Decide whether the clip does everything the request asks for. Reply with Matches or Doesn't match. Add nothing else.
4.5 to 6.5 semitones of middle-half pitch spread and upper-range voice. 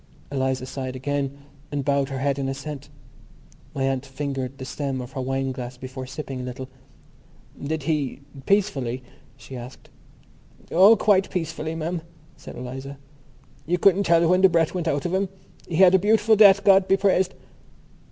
Doesn't match